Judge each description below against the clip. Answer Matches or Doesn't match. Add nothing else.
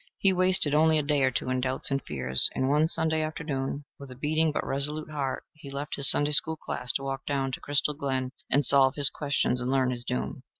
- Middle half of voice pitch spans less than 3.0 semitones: Matches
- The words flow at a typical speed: Doesn't match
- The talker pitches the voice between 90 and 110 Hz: Doesn't match